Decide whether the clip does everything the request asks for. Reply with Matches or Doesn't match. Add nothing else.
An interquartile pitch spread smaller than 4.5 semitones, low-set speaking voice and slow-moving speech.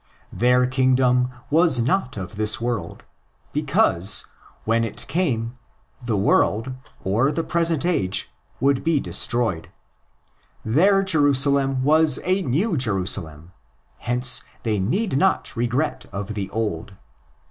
Doesn't match